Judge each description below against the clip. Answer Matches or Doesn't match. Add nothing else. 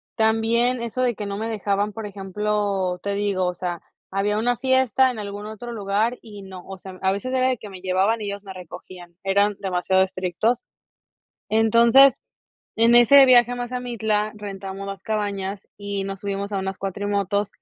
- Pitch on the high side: Matches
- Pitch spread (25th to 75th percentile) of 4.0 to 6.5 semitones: Doesn't match